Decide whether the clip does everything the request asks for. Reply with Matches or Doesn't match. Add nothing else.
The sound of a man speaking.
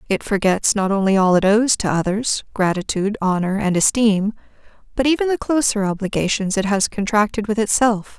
Doesn't match